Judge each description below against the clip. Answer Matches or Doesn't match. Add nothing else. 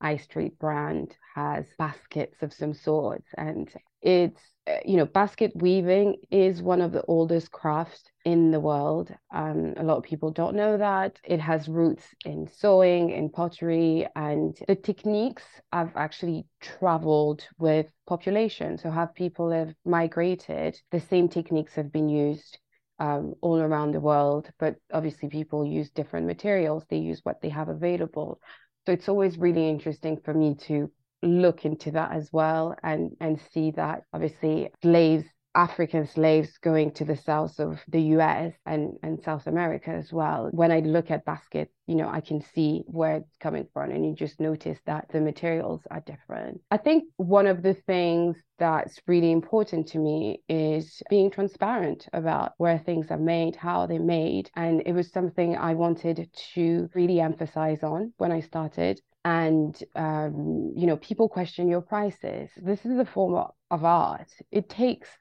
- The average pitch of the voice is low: Doesn't match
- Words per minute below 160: Doesn't match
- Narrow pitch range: Matches